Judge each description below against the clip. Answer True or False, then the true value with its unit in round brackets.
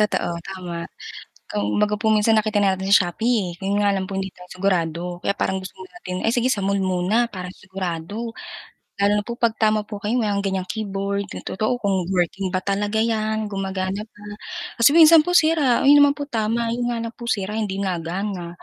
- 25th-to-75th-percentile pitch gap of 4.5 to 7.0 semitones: False (2.9 semitones)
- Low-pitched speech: False (200 Hz)